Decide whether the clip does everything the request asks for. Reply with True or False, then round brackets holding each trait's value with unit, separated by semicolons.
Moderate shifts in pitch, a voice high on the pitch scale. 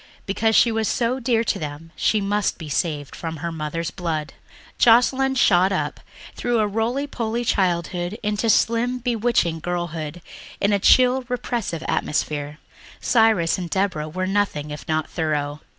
False (6.1 semitones; 195 Hz)